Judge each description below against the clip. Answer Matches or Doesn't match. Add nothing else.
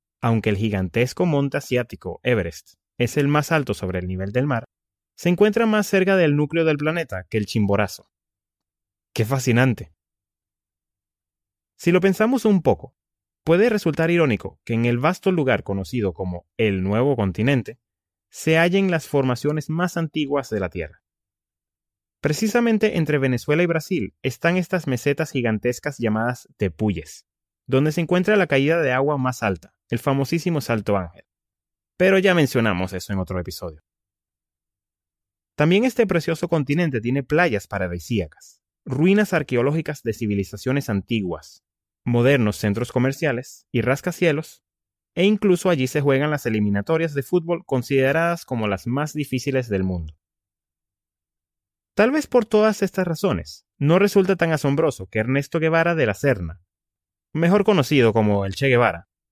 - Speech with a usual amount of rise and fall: Doesn't match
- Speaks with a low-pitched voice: Matches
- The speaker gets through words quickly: Doesn't match